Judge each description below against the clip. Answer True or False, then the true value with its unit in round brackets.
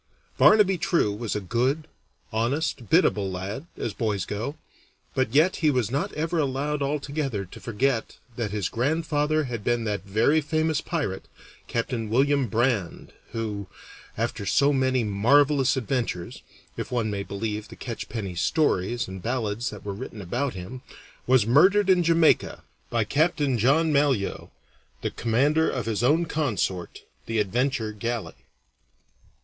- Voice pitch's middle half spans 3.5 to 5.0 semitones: False (5.5 semitones)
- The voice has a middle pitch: False (125 Hz)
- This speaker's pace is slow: False (145 wpm)